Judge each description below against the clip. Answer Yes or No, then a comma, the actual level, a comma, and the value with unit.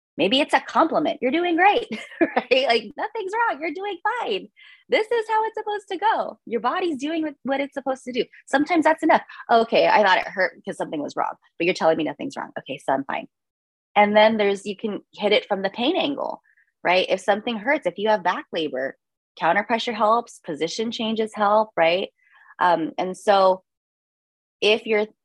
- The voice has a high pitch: Yes, high, 240 Hz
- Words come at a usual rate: Yes, average, 195 wpm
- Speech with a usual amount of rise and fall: No, wide, 8.2 semitones